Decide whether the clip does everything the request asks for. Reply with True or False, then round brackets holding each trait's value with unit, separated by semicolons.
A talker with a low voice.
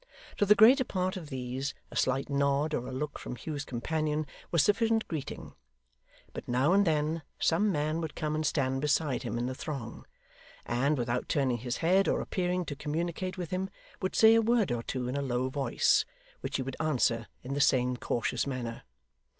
False (145 Hz)